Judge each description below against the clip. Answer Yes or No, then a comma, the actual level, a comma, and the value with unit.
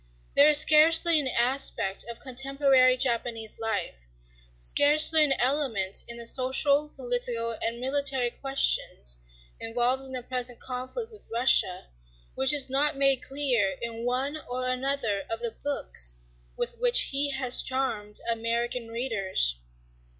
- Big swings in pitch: No, average, 3.1 semitones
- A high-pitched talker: Yes, very high, 255 Hz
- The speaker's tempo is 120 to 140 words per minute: Yes, slow, 135 wpm